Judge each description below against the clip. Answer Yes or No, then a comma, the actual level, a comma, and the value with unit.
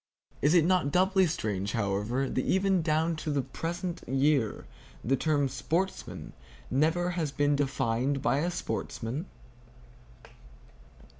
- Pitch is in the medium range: Yes, medium, 145 Hz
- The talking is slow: Yes, slow, 125 wpm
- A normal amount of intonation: Yes, average, 4.6 semitones